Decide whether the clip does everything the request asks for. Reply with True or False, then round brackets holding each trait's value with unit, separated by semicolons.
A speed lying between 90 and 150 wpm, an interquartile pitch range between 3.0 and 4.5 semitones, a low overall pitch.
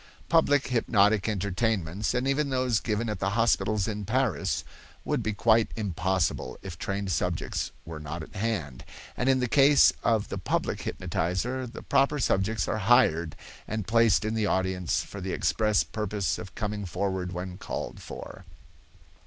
False (160 wpm; 3.7 semitones; 105 Hz)